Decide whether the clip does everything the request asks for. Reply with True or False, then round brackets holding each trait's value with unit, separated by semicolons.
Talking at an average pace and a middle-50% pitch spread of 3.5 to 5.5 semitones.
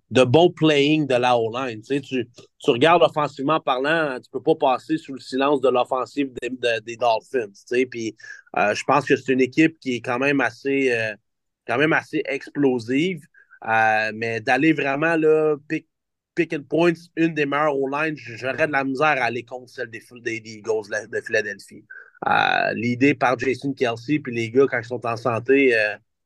True (205 wpm; 4.3 semitones)